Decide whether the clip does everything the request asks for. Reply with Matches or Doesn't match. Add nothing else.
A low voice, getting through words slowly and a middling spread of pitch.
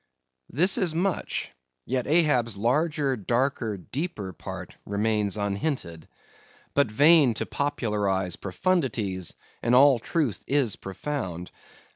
Doesn't match